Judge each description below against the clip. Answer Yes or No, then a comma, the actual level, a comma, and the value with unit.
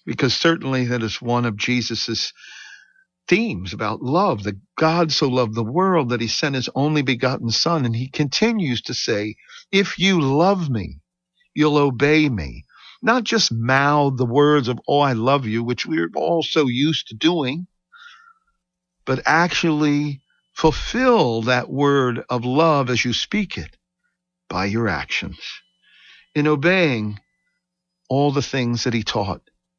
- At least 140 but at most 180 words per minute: Yes, average, 150 wpm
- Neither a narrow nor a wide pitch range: No, wide, 6.7 semitones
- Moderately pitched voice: Yes, medium, 145 Hz